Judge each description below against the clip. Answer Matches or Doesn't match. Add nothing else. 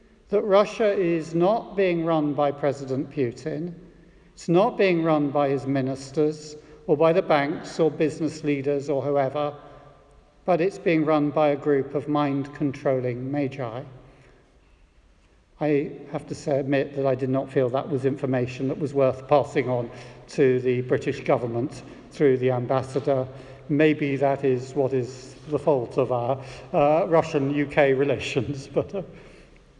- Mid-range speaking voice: Matches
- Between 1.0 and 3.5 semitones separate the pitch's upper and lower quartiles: Matches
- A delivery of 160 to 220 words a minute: Doesn't match